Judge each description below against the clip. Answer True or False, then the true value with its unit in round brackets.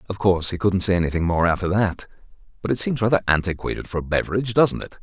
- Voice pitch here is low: True (95 Hz)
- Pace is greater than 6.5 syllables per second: True (7.1 syllables/s)